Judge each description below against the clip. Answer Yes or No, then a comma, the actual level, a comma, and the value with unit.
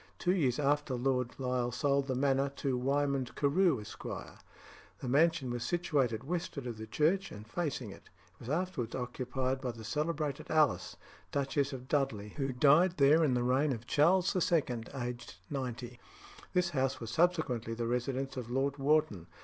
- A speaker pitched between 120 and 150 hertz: Yes, low, 135 Hz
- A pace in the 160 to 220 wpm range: Yes, average, 165 wpm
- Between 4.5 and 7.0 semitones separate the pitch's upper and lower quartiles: No, average, 3.5 semitones